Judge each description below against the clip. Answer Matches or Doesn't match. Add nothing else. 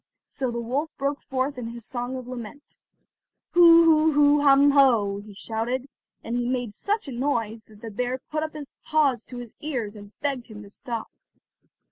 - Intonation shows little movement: Doesn't match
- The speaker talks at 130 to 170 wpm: Doesn't match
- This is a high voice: Matches